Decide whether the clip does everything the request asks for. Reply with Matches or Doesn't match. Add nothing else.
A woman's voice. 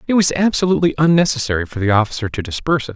Doesn't match